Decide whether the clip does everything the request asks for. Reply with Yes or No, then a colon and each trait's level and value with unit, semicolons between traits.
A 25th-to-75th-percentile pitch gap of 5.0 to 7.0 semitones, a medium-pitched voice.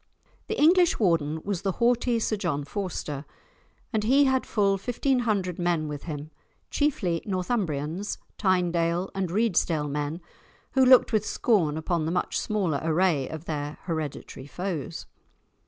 Yes: average, 5.3 semitones; medium, 180 Hz